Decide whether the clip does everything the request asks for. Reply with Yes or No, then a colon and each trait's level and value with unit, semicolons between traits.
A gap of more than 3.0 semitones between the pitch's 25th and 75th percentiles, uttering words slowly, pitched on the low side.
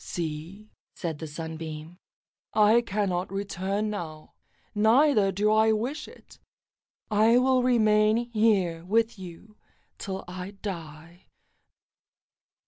No: average, 4.0 semitones; slow, 105 wpm; high, 200 Hz